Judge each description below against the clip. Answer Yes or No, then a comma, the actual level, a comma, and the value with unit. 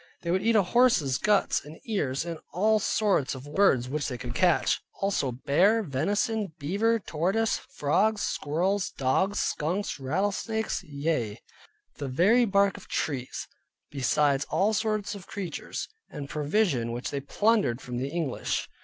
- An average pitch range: No, wide, 6.7 semitones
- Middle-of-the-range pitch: Yes, medium, 170 Hz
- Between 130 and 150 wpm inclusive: Yes, average, 145 wpm